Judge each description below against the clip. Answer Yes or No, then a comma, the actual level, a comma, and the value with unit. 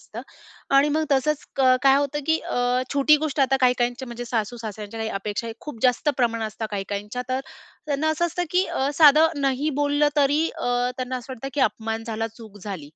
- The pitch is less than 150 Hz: No, very high, 255 Hz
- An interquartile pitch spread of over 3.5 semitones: Yes, average, 4.4 semitones